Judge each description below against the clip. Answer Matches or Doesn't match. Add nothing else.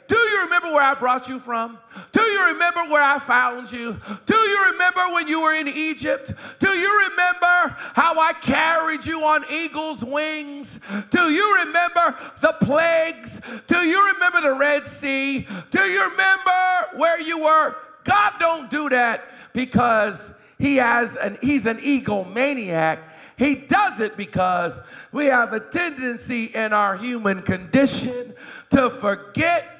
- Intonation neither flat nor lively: Doesn't match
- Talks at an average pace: Matches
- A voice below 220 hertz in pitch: Doesn't match